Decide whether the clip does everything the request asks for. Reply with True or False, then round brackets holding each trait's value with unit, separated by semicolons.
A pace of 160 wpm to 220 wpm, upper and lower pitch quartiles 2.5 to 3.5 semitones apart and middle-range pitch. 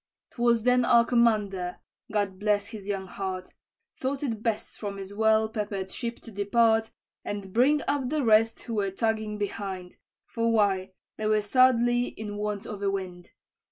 False (165 wpm; 2.8 semitones; 215 Hz)